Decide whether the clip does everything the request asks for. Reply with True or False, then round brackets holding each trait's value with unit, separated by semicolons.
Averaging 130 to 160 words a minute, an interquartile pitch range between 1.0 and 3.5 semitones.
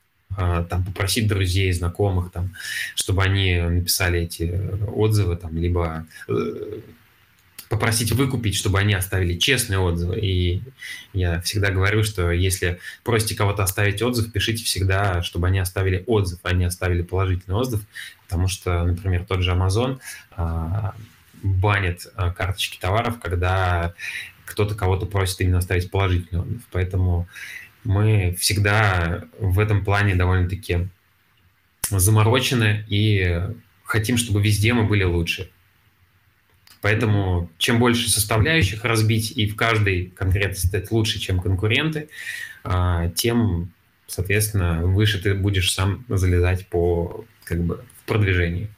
False (120 wpm; 2.9 semitones)